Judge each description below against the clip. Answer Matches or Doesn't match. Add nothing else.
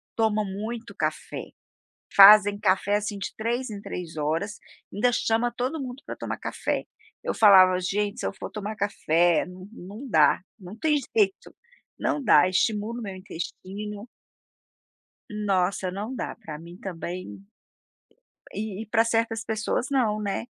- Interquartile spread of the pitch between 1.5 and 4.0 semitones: Matches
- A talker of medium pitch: Doesn't match